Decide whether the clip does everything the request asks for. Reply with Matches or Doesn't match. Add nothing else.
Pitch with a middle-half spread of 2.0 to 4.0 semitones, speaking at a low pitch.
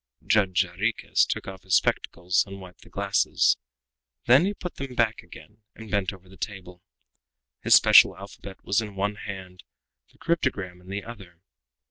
Matches